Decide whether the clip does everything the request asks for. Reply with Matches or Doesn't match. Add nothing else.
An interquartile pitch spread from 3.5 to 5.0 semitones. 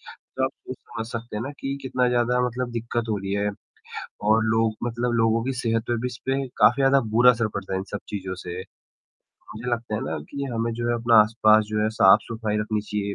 Doesn't match